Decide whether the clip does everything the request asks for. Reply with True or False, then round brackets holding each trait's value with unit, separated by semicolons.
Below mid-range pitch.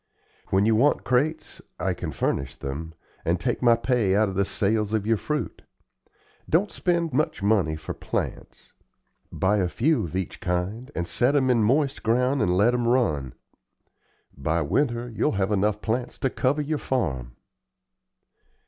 True (110 Hz)